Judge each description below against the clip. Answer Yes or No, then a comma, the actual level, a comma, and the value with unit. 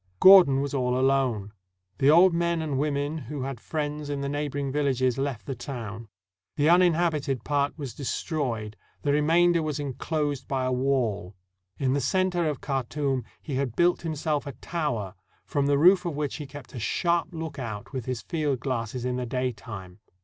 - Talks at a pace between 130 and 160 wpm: No, average, 175 wpm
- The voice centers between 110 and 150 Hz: Yes, medium, 140 Hz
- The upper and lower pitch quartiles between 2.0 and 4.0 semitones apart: Yes, average, 3.3 semitones